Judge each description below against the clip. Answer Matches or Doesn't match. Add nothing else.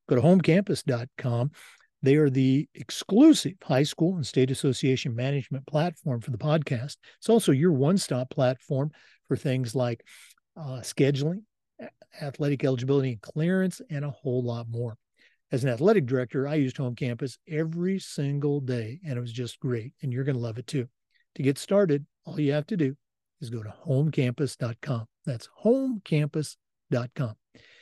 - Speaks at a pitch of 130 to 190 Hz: Matches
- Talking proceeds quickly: Doesn't match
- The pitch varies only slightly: Doesn't match